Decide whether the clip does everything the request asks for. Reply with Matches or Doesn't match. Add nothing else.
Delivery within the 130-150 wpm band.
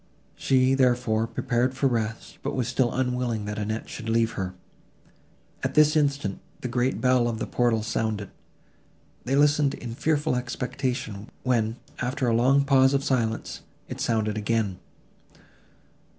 Matches